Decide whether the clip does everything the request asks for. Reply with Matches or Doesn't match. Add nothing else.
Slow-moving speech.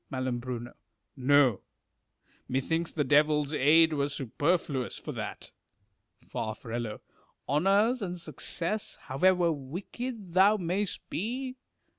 Matches